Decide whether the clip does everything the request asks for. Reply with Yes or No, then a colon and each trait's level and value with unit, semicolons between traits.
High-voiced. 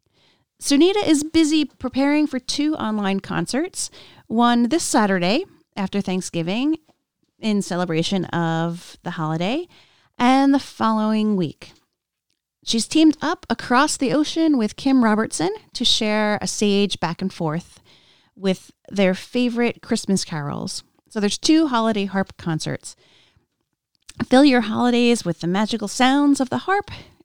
Yes: high, 225 Hz